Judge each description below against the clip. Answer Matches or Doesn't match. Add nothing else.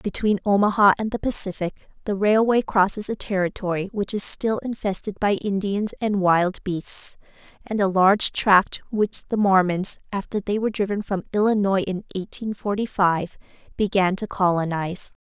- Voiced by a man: Doesn't match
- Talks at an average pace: Matches